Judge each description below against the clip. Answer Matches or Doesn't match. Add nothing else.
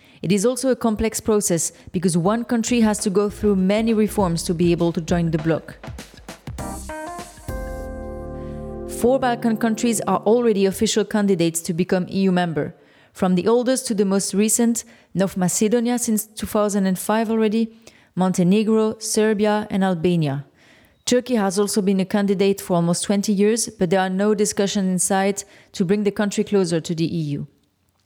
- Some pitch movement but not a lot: Matches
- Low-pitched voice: Doesn't match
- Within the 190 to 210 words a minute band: Doesn't match